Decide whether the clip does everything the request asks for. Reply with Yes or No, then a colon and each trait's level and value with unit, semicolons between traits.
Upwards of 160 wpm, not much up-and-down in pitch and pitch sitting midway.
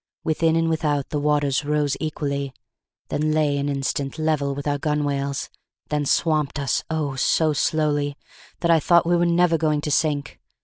Yes: average, 170 wpm; narrow, 1.9 semitones; medium, 150 Hz